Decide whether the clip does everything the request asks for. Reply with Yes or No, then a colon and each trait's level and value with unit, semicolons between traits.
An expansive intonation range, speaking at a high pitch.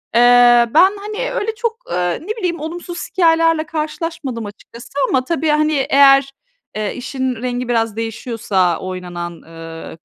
Yes: wide, 6.5 semitones; very high, 265 Hz